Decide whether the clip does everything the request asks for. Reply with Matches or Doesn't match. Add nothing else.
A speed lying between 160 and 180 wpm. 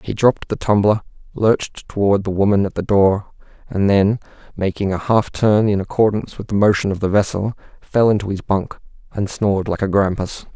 Doesn't match